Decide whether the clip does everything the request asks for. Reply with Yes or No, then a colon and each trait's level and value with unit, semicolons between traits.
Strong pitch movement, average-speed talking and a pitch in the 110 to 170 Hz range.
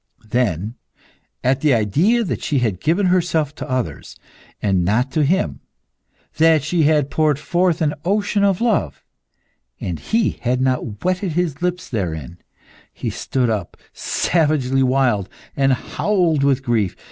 Yes: wide, 6.5 semitones; average, 145 wpm; medium, 140 Hz